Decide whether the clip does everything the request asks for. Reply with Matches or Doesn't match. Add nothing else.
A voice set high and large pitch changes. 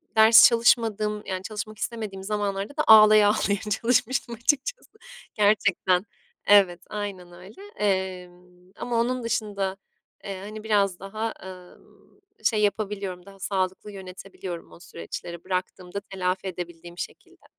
Doesn't match